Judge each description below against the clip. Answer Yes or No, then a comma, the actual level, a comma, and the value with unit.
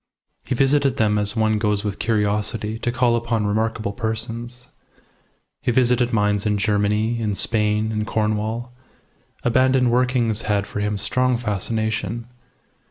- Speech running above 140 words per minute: No, slow, 135 wpm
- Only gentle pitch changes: Yes, narrow, 2.2 semitones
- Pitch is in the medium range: No, low, 110 Hz